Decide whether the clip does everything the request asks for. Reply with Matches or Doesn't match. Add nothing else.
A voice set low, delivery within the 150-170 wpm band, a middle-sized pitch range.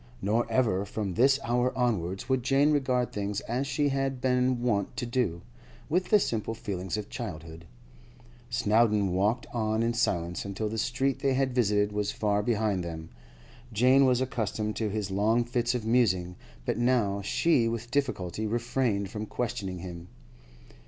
Matches